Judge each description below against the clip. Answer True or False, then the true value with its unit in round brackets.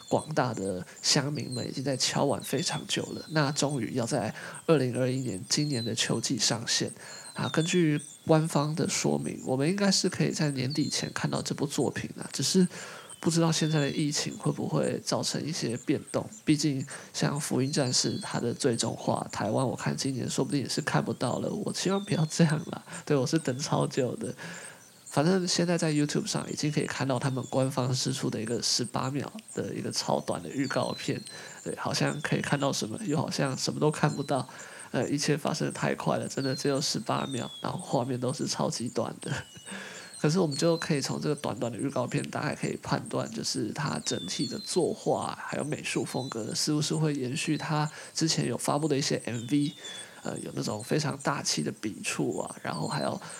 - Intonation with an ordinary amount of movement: True (3.1 semitones)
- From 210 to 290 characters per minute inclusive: False (305 characters per minute)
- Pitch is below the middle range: False (150 Hz)